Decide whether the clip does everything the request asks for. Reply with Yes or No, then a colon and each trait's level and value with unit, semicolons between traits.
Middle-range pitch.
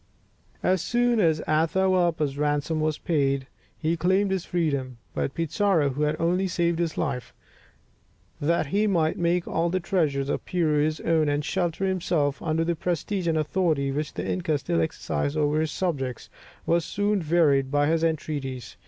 Yes: medium, 160 Hz